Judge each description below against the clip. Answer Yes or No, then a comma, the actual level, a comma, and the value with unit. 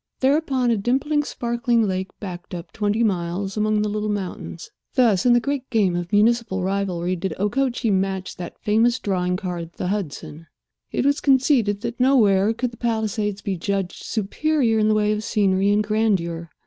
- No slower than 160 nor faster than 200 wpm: Yes, average, 175 wpm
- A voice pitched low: No, high, 210 Hz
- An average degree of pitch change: Yes, average, 3.8 semitones